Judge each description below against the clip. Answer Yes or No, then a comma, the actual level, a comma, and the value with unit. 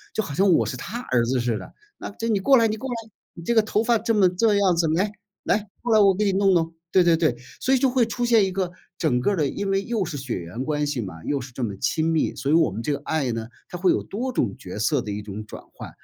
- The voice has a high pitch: No, medium, 175 Hz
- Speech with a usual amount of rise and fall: No, wide, 8.6 semitones